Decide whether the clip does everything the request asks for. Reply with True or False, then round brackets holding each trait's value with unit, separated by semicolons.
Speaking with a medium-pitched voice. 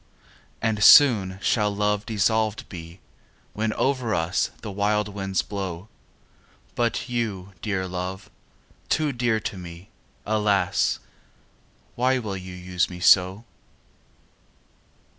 False (100 Hz)